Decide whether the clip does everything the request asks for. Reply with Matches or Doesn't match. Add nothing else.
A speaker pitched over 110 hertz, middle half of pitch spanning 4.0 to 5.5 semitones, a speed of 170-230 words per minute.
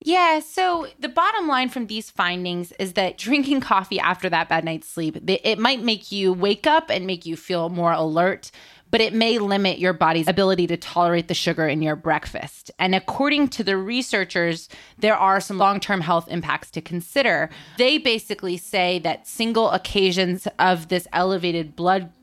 Matches